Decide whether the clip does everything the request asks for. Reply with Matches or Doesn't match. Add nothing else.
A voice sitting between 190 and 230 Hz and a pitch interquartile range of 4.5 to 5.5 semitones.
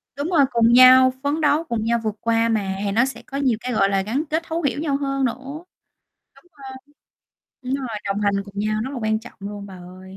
Doesn't match